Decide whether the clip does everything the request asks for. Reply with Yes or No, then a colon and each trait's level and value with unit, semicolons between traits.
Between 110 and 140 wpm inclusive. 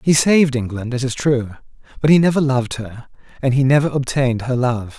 No: fast, 205 wpm